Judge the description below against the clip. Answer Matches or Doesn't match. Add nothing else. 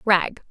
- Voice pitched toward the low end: Doesn't match